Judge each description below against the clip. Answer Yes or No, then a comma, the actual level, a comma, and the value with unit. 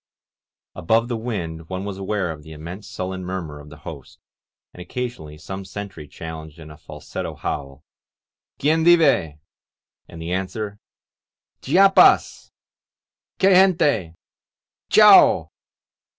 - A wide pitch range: Yes, wide, 6.0 semitones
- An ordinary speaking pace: No, slow, 120 wpm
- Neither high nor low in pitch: No, very low, 95 Hz